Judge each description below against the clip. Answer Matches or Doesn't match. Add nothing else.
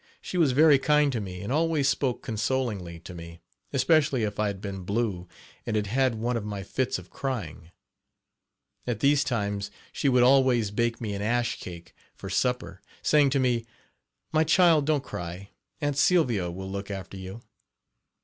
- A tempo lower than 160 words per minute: Doesn't match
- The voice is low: Matches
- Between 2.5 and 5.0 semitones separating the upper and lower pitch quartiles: Doesn't match